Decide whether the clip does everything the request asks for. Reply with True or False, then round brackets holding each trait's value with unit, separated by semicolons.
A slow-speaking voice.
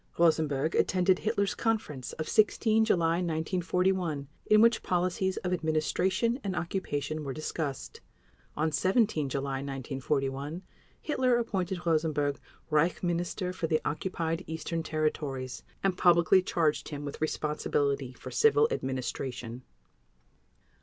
True (115 wpm)